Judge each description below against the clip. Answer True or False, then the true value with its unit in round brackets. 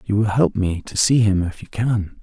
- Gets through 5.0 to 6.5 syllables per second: False (4.8 syllables/s)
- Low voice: True (100 Hz)